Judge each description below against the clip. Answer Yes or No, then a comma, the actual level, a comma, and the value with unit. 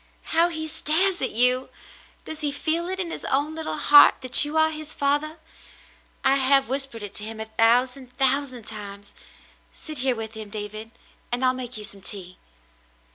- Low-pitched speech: No, very high, 260 Hz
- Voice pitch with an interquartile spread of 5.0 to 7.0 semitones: Yes, wide, 5.5 semitones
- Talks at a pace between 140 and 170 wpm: No, average, 185 wpm